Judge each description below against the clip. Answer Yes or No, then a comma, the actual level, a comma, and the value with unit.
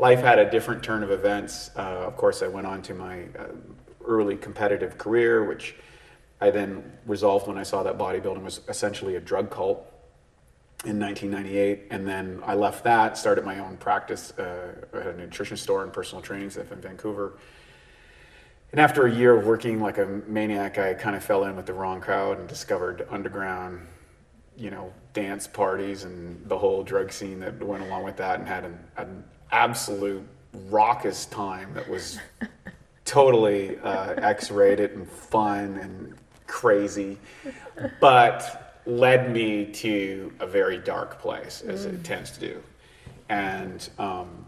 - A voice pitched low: Yes, low, 100 Hz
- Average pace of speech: Yes, average, 165 wpm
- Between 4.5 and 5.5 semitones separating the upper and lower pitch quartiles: No, average, 3.8 semitones